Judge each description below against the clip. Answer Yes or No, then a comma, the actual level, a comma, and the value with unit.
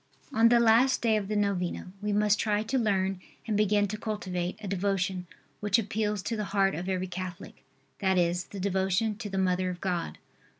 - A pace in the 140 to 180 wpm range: No, average, 200 wpm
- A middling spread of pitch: No, narrow, 2.3 semitones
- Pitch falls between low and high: No, high, 200 Hz